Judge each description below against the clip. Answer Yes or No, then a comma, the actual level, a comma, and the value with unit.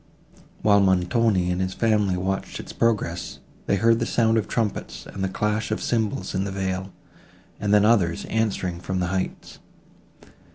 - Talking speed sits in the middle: Yes, average, 165 wpm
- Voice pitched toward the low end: Yes, low, 100 Hz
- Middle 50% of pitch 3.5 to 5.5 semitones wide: No, average, 2.9 semitones